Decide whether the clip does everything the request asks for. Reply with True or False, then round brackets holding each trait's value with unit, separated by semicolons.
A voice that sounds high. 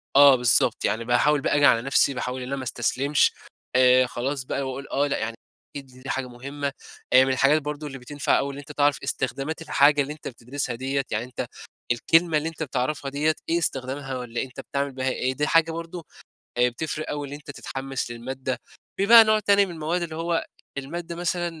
False (140 Hz)